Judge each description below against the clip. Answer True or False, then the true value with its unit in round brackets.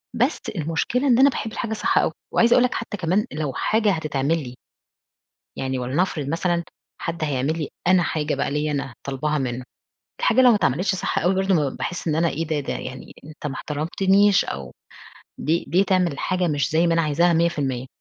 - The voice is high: False (165 Hz)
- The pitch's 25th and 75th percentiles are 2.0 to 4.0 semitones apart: False (4.6 semitones)